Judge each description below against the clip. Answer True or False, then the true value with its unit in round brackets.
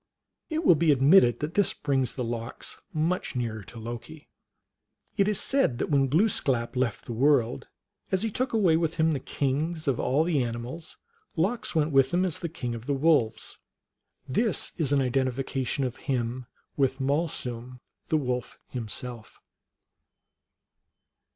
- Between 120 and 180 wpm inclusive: True (150 wpm)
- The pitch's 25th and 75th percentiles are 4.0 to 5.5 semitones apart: True (4.7 semitones)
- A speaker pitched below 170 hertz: True (135 Hz)